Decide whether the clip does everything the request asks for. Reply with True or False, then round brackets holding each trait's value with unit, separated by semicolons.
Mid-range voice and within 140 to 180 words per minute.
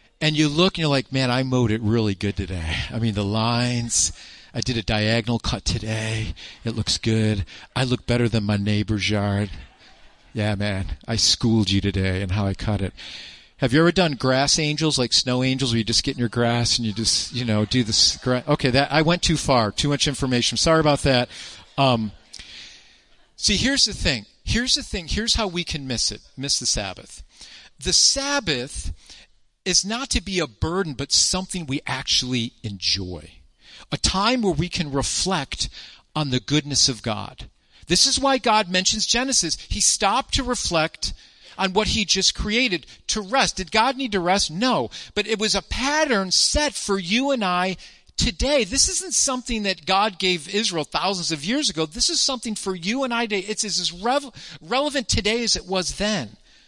False (145 Hz; 195 wpm)